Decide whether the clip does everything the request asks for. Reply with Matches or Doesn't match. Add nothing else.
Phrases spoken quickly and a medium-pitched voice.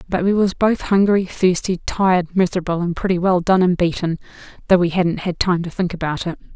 Matches